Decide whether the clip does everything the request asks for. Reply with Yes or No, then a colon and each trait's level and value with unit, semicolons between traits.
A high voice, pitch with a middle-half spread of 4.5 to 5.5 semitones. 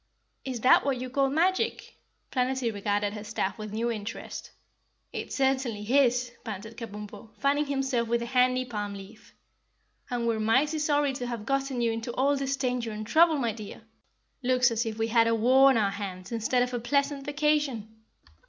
No: high, 245 Hz; average, 3.6 semitones